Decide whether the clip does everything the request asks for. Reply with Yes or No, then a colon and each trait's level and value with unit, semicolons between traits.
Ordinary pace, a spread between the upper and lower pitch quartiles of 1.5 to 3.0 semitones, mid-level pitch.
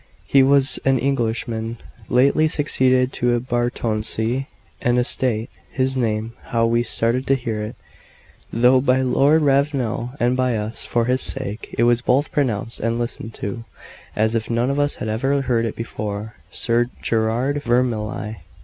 No: average, 160 wpm; narrow, 2.6 semitones; low, 120 Hz